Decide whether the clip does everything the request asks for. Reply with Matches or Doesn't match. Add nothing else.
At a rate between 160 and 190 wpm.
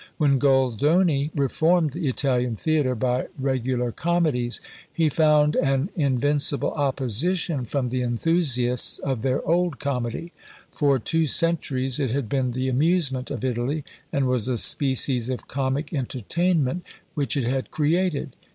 Doesn't match